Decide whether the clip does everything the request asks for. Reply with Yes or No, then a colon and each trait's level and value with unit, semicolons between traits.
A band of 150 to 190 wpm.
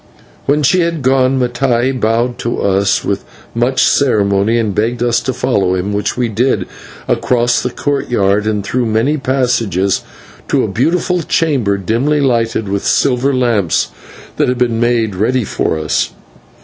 Yes: average, 155 wpm